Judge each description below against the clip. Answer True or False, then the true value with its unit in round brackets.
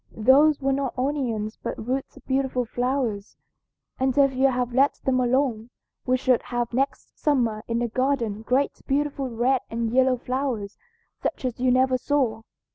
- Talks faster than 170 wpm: False (165 wpm)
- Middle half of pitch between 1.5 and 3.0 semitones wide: True (2.4 semitones)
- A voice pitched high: True (255 Hz)